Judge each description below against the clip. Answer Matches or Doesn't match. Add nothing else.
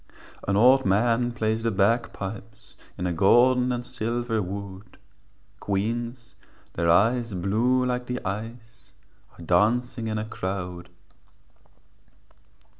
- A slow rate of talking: Matches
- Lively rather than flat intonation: Doesn't match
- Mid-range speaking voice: Doesn't match